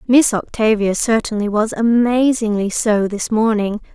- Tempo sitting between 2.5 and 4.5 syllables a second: Yes, 4.4 syllables/s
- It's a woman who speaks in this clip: Yes, female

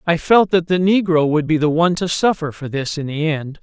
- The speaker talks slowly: No, fast, 265 wpm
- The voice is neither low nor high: Yes, medium, 165 Hz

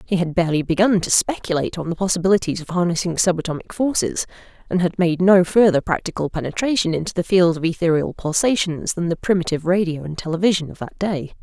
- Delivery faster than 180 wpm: Yes, average, 190 wpm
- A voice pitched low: No, medium, 175 Hz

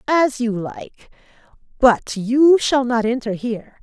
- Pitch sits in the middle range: No, high, 240 Hz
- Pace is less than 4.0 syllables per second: Yes, 3.7 syllables/s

